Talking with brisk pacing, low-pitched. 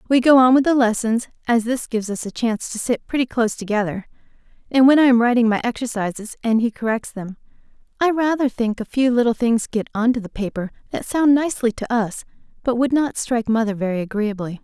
No: fast, 215 wpm; high, 235 Hz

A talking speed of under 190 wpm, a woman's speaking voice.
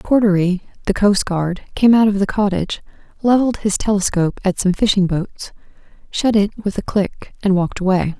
Yes: average, 170 wpm; female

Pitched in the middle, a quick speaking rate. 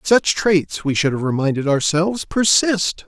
No: medium, 170 Hz; average, 155 wpm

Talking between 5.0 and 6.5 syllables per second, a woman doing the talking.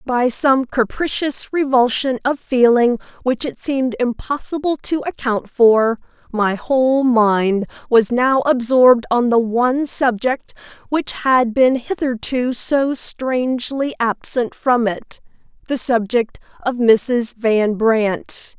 No: 3.6 syllables/s; female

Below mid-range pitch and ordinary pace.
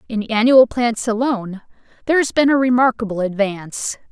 No: high, 230 Hz; average, 145 wpm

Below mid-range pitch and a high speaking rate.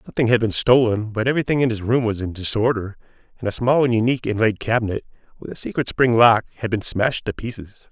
Yes: low, 115 Hz; fast, 220 wpm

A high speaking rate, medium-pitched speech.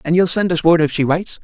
Yes: fast, 335 wpm; medium, 170 Hz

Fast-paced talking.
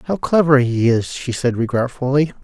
No: average, 170 wpm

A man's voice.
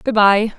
No: female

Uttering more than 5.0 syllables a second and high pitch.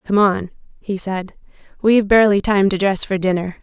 Yes: 5.6 syllables/s; high, 195 Hz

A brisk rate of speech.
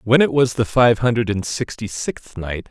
Yes: fast, 220 wpm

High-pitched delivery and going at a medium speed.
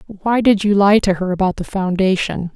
No: high, 195 Hz; fast, 210 wpm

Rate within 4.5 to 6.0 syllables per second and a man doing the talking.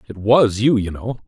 Yes: 4.9 syllables/s; male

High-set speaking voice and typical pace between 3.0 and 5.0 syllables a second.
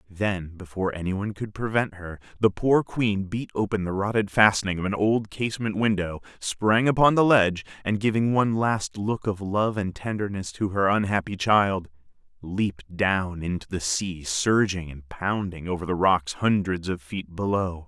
No: low, 100 Hz; 4.7 syllables/s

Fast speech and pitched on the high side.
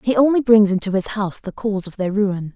Yes: fast, 260 wpm; high, 205 Hz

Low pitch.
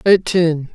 No: medium, 170 Hz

